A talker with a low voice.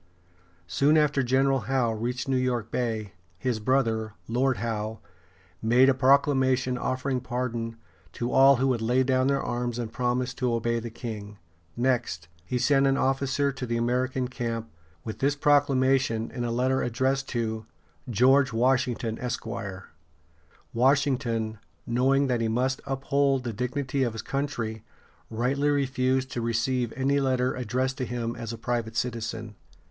Yes: low, 125 Hz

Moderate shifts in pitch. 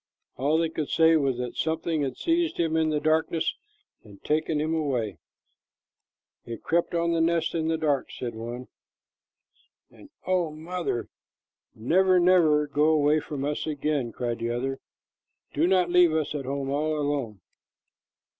Yes: average, 3.2 semitones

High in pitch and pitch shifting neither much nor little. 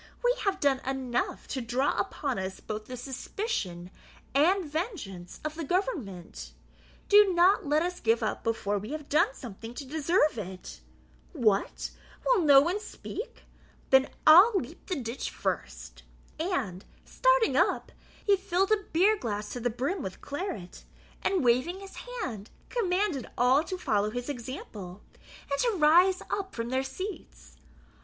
No: very high, 280 Hz; wide, 8.5 semitones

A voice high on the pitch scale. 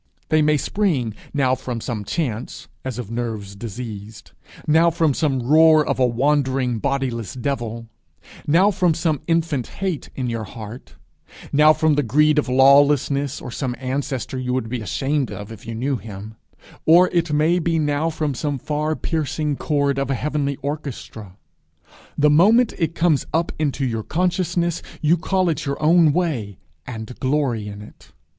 No: medium, 140 Hz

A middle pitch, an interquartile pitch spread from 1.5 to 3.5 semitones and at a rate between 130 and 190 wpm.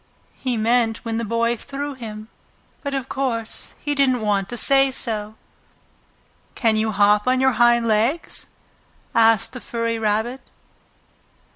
No: high, 230 Hz; average, 3.0 semitones; average, 140 wpm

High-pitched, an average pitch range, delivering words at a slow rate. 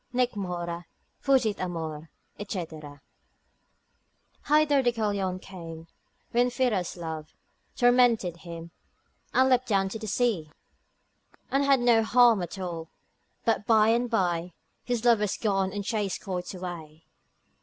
No: high, 200 Hz; wide, 5.8 semitones; slow, 125 wpm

